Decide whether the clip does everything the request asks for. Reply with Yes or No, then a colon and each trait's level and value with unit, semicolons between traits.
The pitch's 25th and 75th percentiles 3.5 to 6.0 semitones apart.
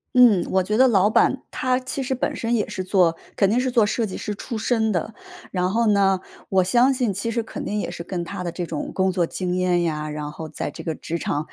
Yes: average, 4.5 semitones